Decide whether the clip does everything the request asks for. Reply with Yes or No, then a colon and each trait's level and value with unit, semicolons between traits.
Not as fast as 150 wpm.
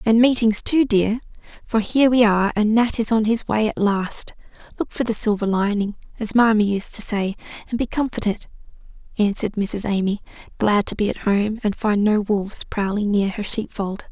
No: average, 190 wpm